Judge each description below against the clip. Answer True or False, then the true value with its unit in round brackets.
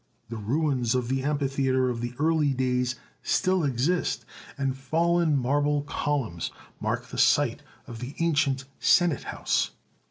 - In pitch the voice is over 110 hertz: True (135 Hz)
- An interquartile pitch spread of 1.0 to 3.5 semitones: True (3.0 semitones)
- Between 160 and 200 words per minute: False (135 wpm)